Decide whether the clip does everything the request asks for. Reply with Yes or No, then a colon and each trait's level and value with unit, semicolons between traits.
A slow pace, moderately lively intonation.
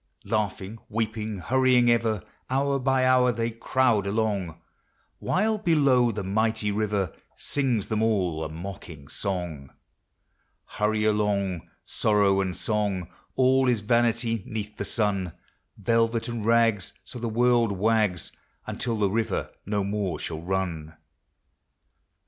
Yes: slow, 125 wpm; average, 3.2 semitones